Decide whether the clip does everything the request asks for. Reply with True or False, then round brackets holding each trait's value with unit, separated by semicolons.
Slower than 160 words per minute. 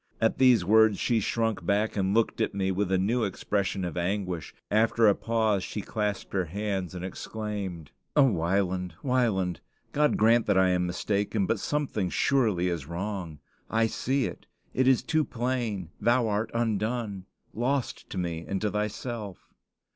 False (165 wpm)